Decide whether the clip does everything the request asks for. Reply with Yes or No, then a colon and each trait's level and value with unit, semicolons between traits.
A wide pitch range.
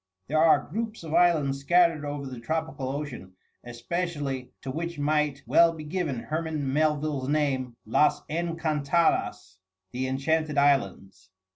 No: average, 3.3 semitones